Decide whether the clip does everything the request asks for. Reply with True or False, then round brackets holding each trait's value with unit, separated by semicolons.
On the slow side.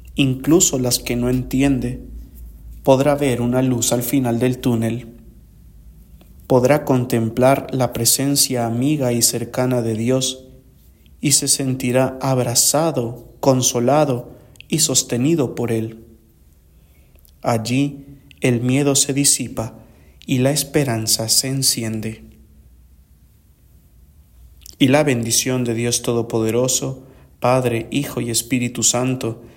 True (105 wpm)